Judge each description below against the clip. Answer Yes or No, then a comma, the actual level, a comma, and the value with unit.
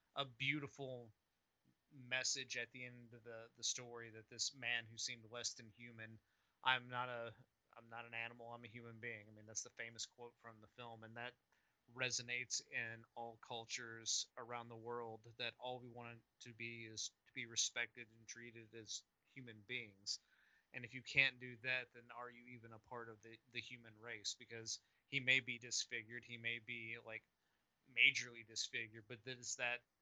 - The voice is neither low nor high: No, low, 120 Hz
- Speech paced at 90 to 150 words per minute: No, average, 190 wpm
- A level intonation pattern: Yes, narrow, 1.4 semitones